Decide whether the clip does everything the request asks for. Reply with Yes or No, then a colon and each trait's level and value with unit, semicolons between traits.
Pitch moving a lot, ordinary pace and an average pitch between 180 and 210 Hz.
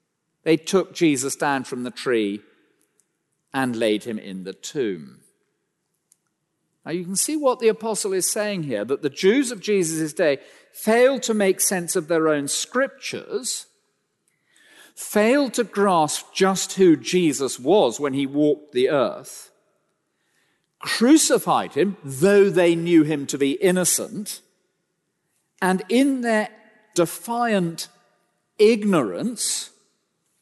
No: wide, 5.8 semitones; slow, 125 wpm; medium, 185 Hz